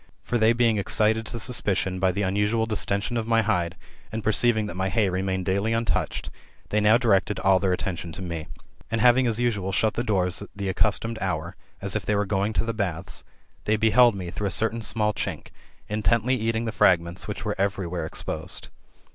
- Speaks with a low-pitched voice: Yes, low, 105 Hz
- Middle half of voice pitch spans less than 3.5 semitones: Yes, average, 3.0 semitones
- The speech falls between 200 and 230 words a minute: Yes, fast, 205 wpm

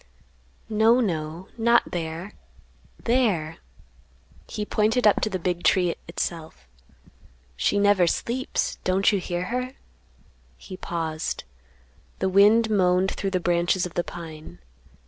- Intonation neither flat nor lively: Yes, average, 3.8 semitones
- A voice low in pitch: No, medium, 185 Hz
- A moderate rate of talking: No, slow, 125 wpm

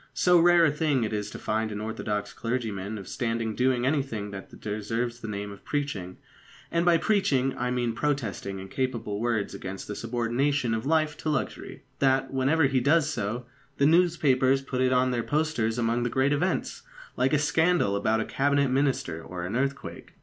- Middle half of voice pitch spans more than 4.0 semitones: Yes, average, 4.5 semitones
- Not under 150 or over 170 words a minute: No, average, 185 wpm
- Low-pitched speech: Yes, low, 125 Hz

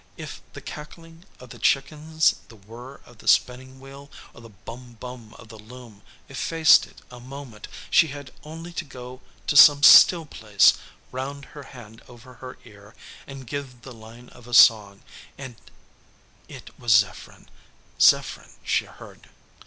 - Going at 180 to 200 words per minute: No, average, 160 wpm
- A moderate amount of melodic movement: Yes, average, 3.6 semitones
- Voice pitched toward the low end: Yes, low, 125 Hz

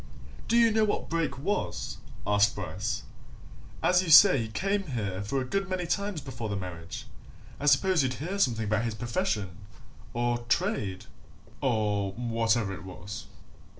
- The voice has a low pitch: Yes, low, 120 Hz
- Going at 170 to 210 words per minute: No, average, 155 wpm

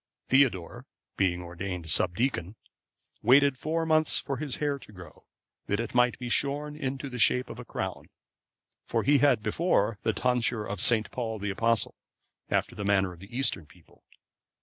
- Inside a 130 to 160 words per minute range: No, average, 170 wpm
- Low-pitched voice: Yes, low, 120 Hz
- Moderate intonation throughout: No, wide, 5.7 semitones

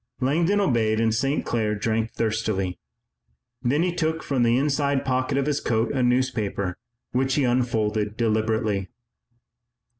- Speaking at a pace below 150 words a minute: Yes, average, 140 wpm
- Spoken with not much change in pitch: No, average, 3.8 semitones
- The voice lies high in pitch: No, low, 120 Hz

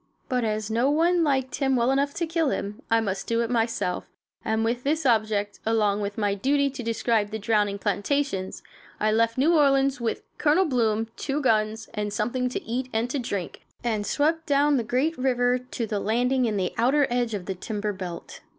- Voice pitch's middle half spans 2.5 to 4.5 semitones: Yes, average, 4.2 semitones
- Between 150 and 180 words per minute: No, fast, 205 wpm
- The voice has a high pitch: Yes, high, 235 Hz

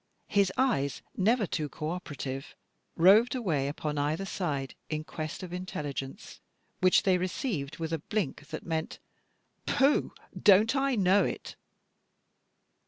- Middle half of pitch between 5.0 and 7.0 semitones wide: Yes, average, 5.3 semitones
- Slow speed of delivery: Yes, slow, 130 wpm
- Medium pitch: Yes, medium, 175 Hz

